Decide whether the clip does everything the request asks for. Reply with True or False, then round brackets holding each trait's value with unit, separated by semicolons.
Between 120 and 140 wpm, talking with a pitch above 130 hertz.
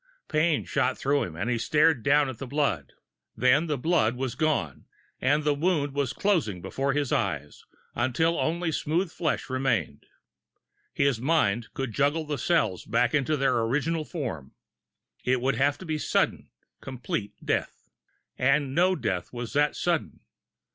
False (155 wpm; 140 Hz)